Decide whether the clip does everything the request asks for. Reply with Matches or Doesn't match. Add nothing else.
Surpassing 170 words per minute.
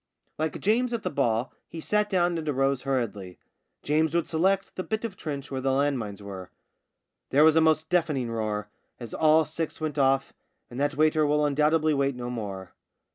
Matches